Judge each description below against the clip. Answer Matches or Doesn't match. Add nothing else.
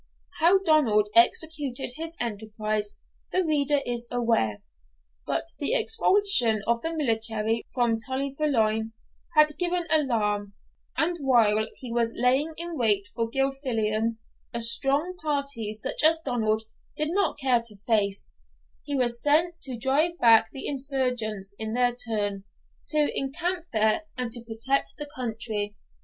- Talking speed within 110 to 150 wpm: Matches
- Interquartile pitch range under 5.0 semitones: Doesn't match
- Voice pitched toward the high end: Matches